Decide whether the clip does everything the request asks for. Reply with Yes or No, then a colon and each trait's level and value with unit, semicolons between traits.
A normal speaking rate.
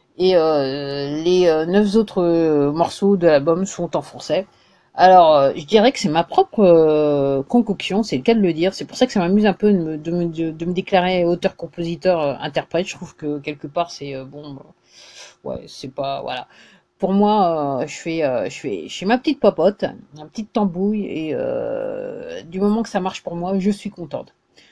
Yes: average, 190 wpm